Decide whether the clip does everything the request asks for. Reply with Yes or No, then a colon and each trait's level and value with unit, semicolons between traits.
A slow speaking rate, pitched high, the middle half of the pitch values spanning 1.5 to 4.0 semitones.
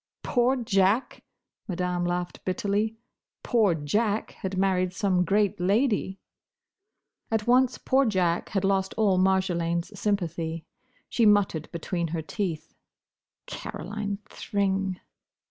Yes: slow, 110 wpm; high, 195 Hz; average, 2.9 semitones